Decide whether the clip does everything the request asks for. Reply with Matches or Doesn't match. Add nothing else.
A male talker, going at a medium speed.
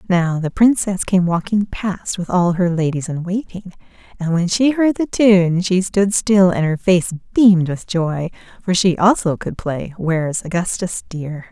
Doesn't match